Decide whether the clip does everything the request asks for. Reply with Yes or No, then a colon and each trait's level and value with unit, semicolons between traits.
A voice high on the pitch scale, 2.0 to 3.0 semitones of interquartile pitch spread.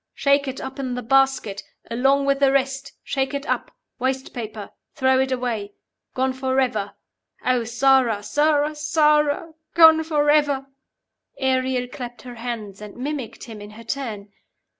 Yes: very high, 265 Hz; narrow, 2.6 semitones